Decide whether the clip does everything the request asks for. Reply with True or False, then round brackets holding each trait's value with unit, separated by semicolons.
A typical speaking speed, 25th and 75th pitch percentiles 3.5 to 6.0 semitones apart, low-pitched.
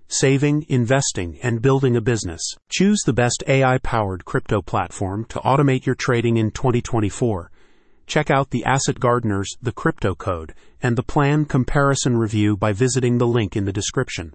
True (165 wpm; 4.2 semitones; 120 Hz)